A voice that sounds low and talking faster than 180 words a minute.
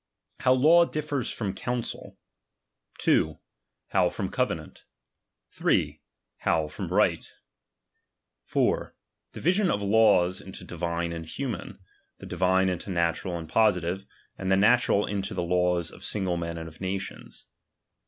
No: very low, 95 Hz; slow, 135 wpm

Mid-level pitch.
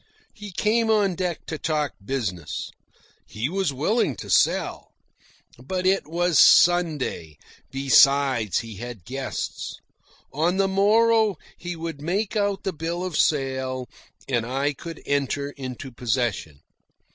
Yes: medium, 150 Hz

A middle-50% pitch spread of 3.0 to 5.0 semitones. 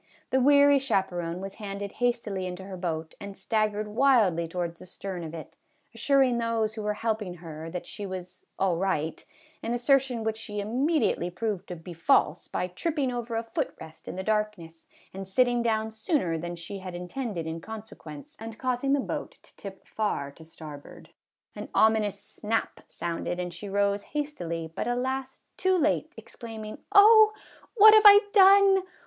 No: wide, 5.5 semitones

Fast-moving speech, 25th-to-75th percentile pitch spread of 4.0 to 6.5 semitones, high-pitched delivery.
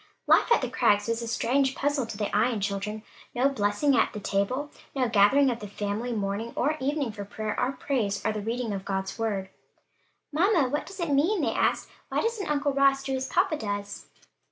Yes: fast, 210 wpm; average, 5.3 semitones; high, 240 Hz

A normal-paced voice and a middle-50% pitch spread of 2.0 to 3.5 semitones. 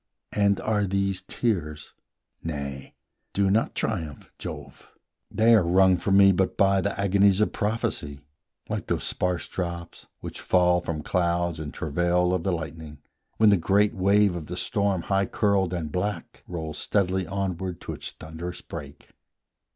Yes: average, 155 wpm; average, 2.8 semitones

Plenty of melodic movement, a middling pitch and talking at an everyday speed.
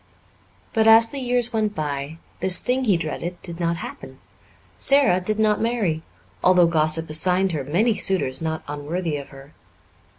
Yes: wide, 5.8 semitones; medium, 180 Hz; average, 160 wpm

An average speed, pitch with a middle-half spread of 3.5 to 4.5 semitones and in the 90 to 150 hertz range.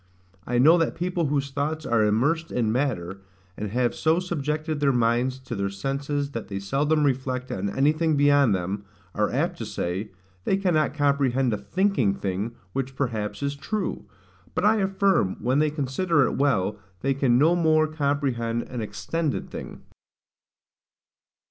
No: average, 160 wpm; average, 5.0 semitones; low, 135 Hz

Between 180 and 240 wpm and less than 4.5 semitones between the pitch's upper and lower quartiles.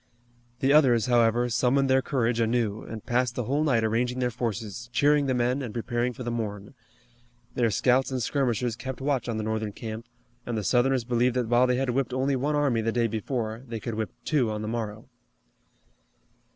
Yes: average, 200 wpm; narrow, 2.4 semitones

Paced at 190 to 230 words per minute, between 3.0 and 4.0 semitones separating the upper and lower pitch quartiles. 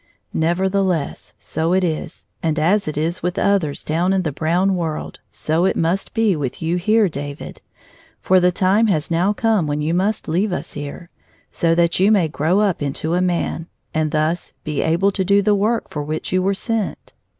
Yes: average, 195 wpm; average, 3.7 semitones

